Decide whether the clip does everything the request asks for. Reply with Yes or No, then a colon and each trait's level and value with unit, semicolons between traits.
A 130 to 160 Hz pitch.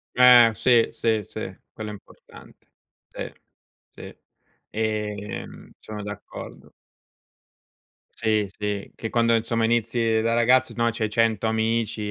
No: low, 110 Hz